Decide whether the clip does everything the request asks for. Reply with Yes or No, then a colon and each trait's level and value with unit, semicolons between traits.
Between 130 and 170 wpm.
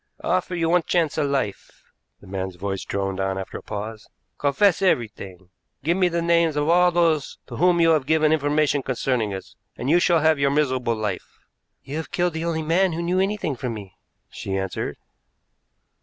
No: average, 195 wpm